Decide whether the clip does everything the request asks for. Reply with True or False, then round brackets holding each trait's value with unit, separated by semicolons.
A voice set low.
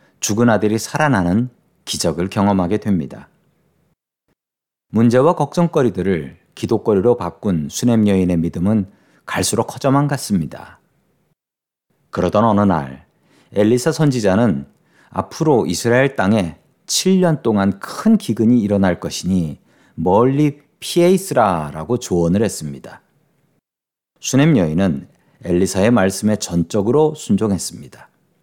True (110 Hz)